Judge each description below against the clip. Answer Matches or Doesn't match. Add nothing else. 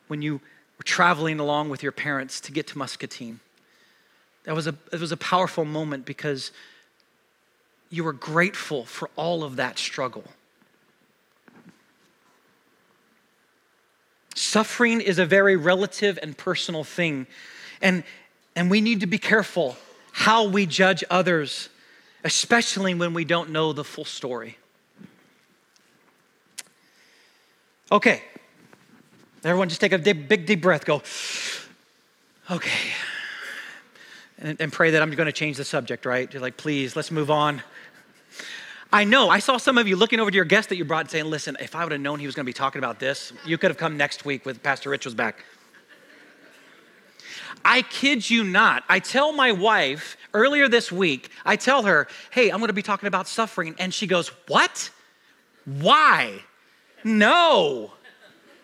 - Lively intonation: Matches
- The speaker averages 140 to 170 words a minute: Matches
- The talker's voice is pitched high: Doesn't match